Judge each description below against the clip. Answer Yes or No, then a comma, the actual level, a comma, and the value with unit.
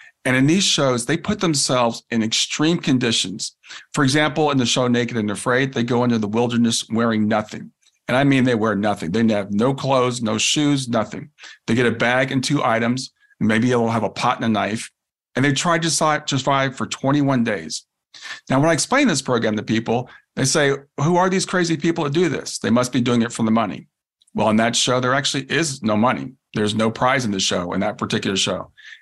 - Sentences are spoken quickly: Yes, fast, 220 wpm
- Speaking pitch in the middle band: No, low, 125 Hz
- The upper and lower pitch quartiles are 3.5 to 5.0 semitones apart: Yes, average, 4.0 semitones